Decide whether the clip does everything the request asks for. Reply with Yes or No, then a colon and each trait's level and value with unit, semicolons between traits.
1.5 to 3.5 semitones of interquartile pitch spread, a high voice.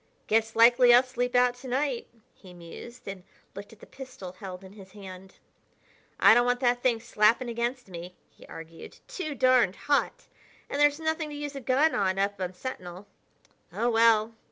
No: average, 4.9 semitones; high, 235 Hz